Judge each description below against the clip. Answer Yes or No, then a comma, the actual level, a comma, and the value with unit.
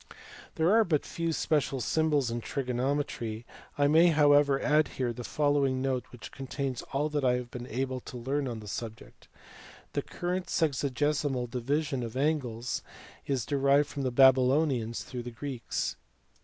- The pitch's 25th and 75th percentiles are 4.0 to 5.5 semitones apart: No, average, 3.0 semitones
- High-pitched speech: No, low, 135 Hz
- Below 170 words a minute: Yes, average, 155 wpm